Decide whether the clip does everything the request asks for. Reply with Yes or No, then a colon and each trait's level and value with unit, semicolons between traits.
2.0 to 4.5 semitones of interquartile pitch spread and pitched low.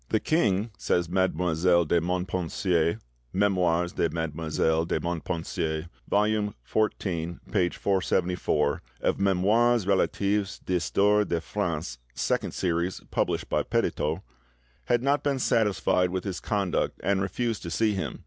Yes: average, 3.3 semitones; very low, 90 Hz